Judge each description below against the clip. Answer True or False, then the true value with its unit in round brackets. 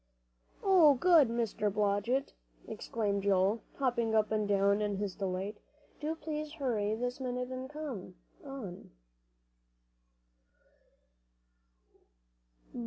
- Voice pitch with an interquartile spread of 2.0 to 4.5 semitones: False (5.0 semitones)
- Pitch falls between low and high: False (230 Hz)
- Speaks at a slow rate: True (100 wpm)